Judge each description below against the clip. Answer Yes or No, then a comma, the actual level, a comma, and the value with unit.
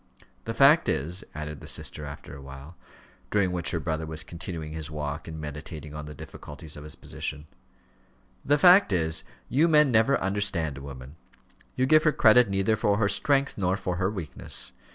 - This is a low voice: Yes, very low, 85 Hz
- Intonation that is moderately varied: No, wide, 6.3 semitones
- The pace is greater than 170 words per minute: Yes, average, 180 wpm